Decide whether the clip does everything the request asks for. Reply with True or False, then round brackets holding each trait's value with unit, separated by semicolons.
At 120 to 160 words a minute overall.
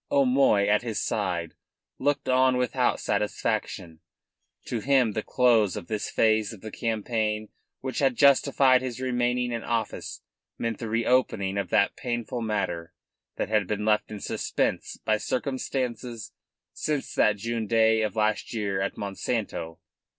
True (145 wpm)